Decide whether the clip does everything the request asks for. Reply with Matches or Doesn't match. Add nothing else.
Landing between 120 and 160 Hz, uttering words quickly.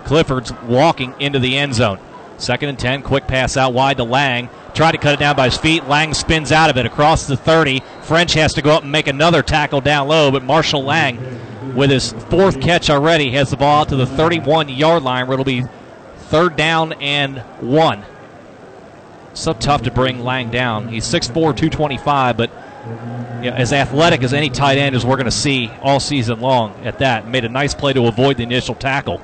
Matches